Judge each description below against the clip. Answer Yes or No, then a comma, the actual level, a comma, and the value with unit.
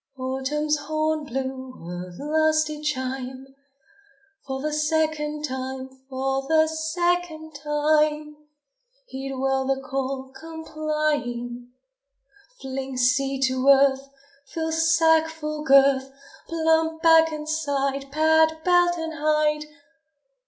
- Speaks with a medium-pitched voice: No, very high, 300 Hz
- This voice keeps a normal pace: No, slow, 105 wpm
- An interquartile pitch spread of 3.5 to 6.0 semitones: No, average, 2.9 semitones